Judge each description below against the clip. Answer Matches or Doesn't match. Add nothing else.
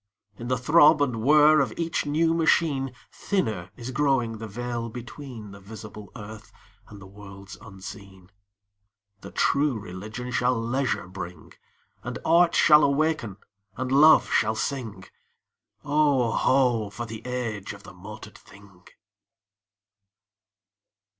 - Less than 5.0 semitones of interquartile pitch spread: Doesn't match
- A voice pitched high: Doesn't match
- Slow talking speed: Matches